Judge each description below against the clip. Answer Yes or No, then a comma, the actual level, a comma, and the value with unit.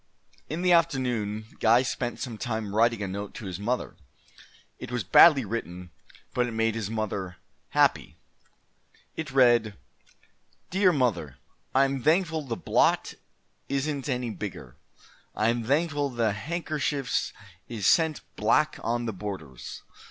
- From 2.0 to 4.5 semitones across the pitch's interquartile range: No, average, 5.0 semitones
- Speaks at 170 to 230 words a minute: No, slow, 135 wpm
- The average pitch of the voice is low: Yes, low, 120 Hz